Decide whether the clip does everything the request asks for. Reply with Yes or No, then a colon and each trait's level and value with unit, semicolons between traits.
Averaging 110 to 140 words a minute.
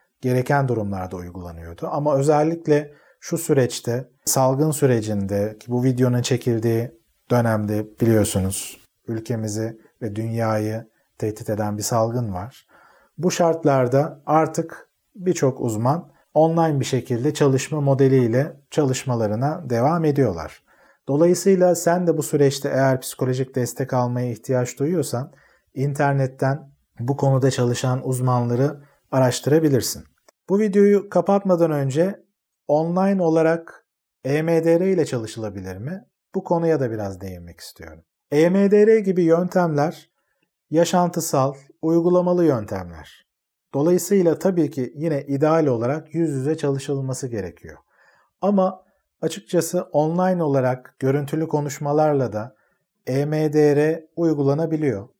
No: average, 100 wpm